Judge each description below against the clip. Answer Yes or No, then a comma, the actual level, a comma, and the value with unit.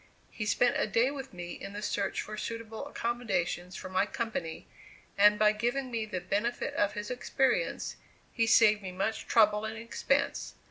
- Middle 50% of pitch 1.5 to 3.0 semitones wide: Yes, average, 2.7 semitones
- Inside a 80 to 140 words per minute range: No, average, 175 wpm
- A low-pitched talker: No, high, 215 Hz